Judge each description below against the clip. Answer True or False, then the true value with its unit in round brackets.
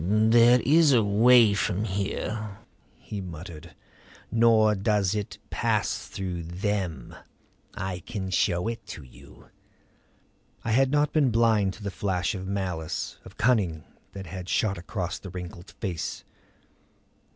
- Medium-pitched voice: False (100 Hz)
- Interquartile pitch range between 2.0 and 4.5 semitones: True (3.7 semitones)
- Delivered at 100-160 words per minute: True (135 wpm)